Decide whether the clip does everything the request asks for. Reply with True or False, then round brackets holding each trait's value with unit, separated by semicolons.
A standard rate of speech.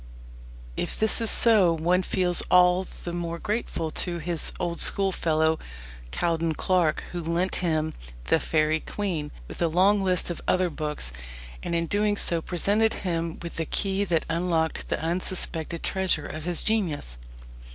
True (155 wpm)